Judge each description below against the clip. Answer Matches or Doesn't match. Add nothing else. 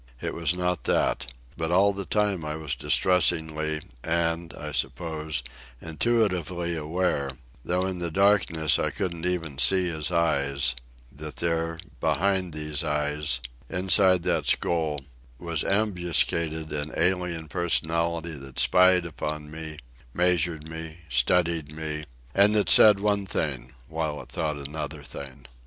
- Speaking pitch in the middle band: Doesn't match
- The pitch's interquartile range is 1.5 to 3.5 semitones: Matches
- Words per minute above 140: Doesn't match